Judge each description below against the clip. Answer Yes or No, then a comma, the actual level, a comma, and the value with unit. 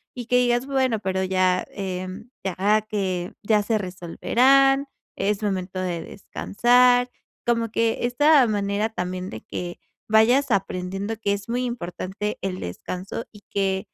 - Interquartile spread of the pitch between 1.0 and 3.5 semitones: No, average, 4.4 semitones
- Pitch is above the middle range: Yes, high, 205 Hz